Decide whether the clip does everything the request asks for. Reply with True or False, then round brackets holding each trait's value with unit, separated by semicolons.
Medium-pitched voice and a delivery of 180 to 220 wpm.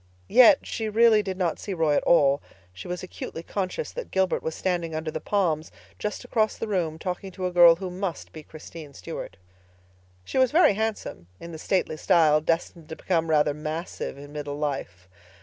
True (170 Hz; 190 wpm)